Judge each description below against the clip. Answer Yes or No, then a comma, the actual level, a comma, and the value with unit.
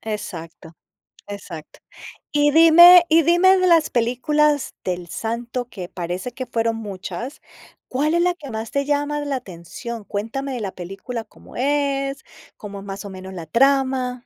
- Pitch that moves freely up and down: Yes, wide, 6.5 semitones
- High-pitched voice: Yes, high, 245 Hz